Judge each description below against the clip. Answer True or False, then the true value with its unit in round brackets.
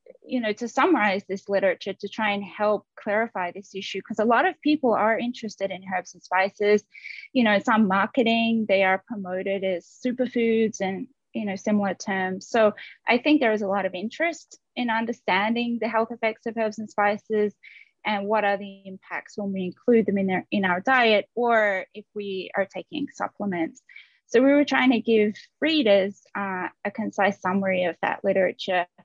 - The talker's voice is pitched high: True (210 Hz)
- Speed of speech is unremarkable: True (185 wpm)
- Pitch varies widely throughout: False (3.1 semitones)